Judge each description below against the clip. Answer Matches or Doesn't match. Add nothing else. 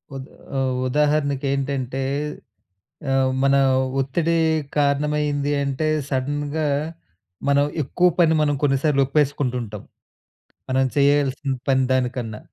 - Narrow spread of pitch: Matches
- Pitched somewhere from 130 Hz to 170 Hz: Matches